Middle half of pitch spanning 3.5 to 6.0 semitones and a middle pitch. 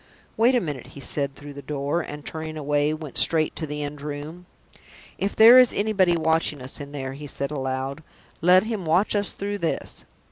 Yes: average, 3.9 semitones; medium, 155 Hz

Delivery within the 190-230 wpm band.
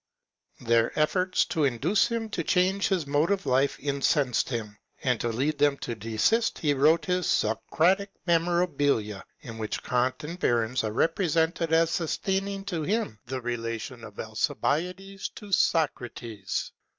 No: average, 155 wpm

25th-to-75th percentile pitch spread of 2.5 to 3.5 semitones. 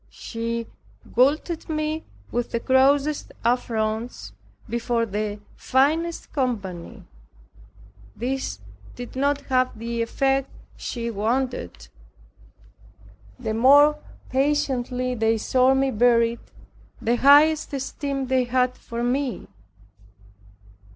Yes: average, 2.9 semitones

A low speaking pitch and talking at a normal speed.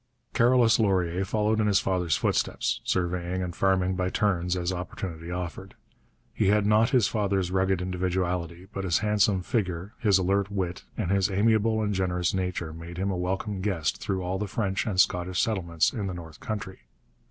Yes: very low, 95 Hz; average, 175 wpm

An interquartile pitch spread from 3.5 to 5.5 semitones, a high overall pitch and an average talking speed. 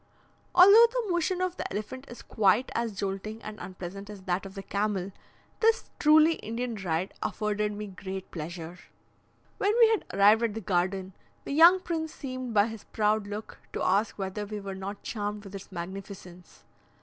Yes: average, 4.6 semitones; high, 210 Hz; average, 175 wpm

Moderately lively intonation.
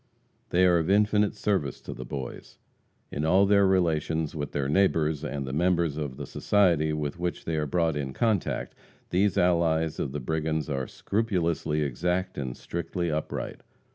Yes: average, 3.6 semitones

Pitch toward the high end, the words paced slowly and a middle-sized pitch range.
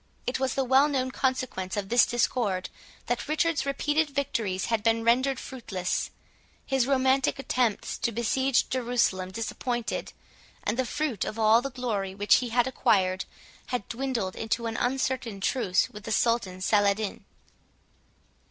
No: high, 240 Hz; average, 145 wpm; average, 3.9 semitones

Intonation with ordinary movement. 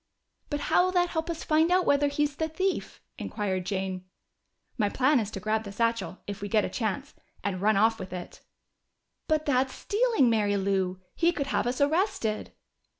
No: wide, 7.5 semitones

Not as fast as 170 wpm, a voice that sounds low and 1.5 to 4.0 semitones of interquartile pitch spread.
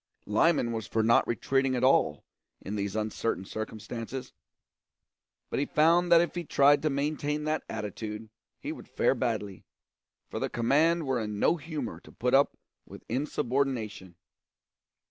No: average, 150 wpm; low, 130 Hz; average, 5.3 semitones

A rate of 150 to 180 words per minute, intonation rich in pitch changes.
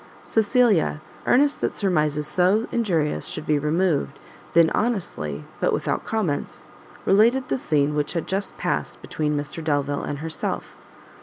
No: average, 140 wpm; wide, 6.0 semitones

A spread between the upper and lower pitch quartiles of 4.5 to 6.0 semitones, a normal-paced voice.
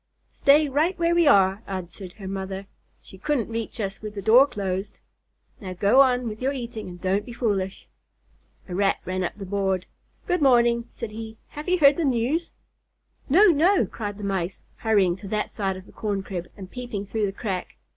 Yes: average, 4.9 semitones; average, 195 wpm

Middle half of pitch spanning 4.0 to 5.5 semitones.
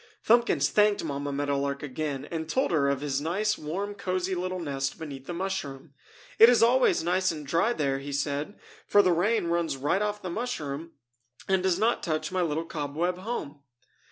Yes: average, 5.2 semitones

